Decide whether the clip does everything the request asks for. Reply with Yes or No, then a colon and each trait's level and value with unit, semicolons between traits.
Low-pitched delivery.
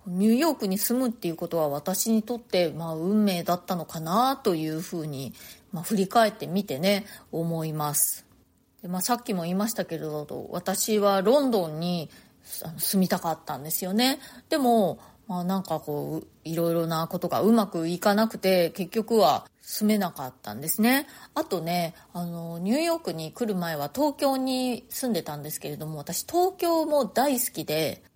No: medium, 185 Hz